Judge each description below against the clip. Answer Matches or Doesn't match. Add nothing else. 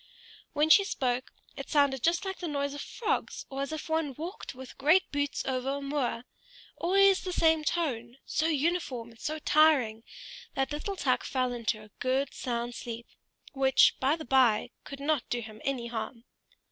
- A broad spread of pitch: Doesn't match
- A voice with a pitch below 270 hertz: Doesn't match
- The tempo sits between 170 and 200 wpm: Matches